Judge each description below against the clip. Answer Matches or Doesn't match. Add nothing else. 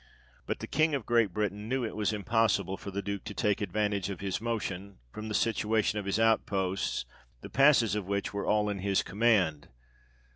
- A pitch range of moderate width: Doesn't match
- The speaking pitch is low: Matches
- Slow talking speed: Doesn't match